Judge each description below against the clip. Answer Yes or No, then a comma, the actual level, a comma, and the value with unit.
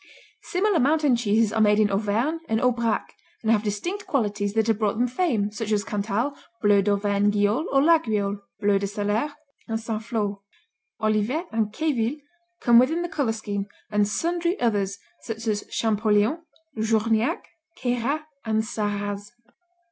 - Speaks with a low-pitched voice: No, high, 220 Hz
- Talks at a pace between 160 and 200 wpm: No, average, 150 wpm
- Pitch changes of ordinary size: Yes, average, 3.3 semitones